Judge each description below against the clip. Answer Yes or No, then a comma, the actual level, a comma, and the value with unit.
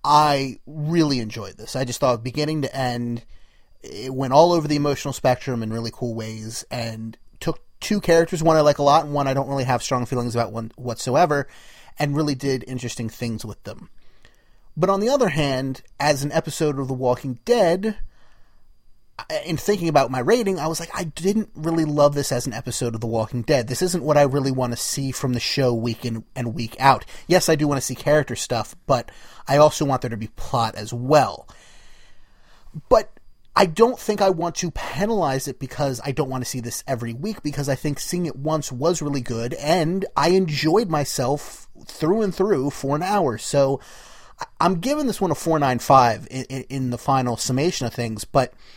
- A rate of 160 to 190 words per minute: No, fast, 205 wpm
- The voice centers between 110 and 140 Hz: Yes, low, 135 Hz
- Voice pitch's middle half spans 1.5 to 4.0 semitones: No, average, 4.5 semitones